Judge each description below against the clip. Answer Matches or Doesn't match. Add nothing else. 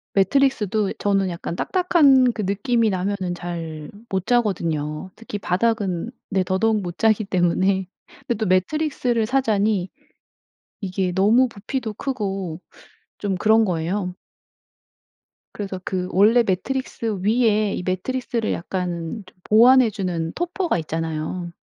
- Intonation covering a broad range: Doesn't match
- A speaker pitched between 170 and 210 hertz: Matches